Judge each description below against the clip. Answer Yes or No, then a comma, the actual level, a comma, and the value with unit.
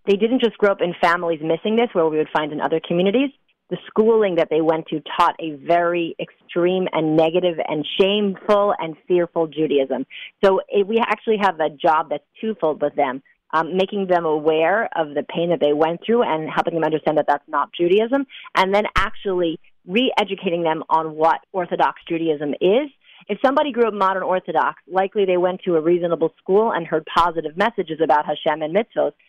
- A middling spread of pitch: Yes, average, 4.1 semitones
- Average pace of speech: Yes, average, 190 wpm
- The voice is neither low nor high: Yes, medium, 170 Hz